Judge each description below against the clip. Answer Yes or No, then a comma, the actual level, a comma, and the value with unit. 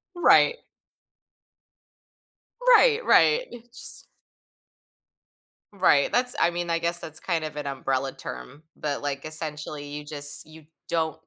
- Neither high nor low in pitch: Yes, medium, 155 Hz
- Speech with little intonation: No, average, 3.1 semitones